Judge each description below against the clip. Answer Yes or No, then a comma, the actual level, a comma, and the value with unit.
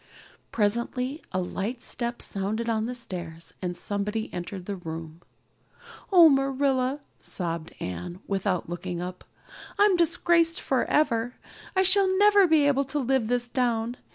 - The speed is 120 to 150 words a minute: Yes, slow, 135 wpm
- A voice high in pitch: Yes, high, 235 Hz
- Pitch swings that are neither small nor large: No, wide, 7.0 semitones